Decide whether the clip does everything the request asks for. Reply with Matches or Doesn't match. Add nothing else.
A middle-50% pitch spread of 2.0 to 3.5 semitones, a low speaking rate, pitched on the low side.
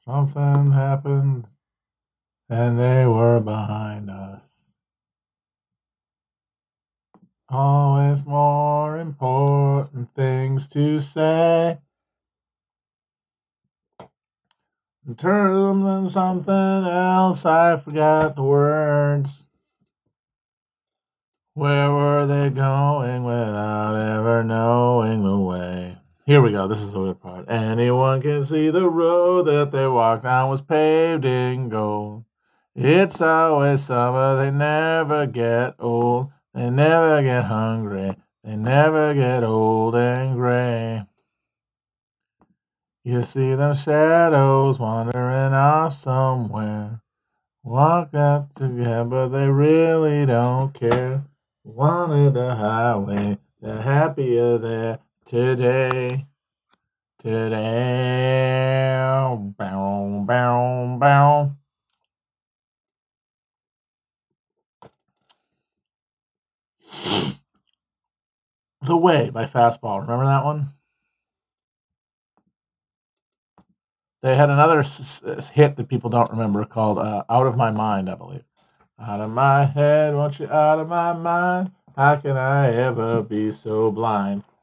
Doesn't match